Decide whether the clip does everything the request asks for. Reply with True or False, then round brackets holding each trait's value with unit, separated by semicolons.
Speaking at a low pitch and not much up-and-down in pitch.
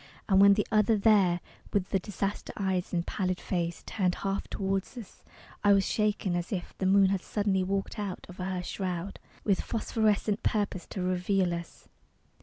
False (195 Hz; 2.0 semitones)